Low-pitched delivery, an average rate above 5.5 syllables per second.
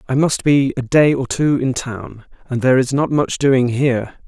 No: low, 130 Hz; 4.7 syllables/s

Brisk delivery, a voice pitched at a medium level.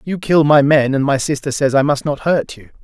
Yes: fast, 275 wpm; medium, 145 Hz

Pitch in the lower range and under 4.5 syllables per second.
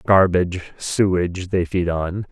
Yes: very low, 90 Hz; 4.3 syllables/s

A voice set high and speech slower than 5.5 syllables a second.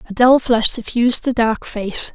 Yes: high, 230 Hz; 4.6 syllables/s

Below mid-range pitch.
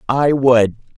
Yes: low, 130 Hz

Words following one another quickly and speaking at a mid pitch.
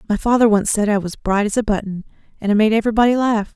No: fast, 255 wpm; high, 215 Hz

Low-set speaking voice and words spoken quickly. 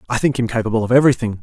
Yes: low, 120 Hz; fast, 255 wpm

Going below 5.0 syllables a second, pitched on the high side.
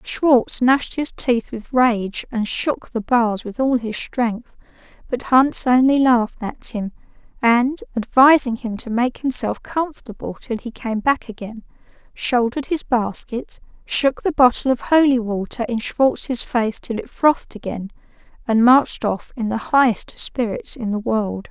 Yes: 4.2 syllables/s; high, 240 Hz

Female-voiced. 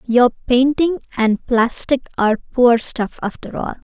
Yes: female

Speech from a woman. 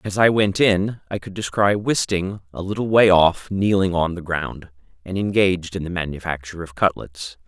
No: male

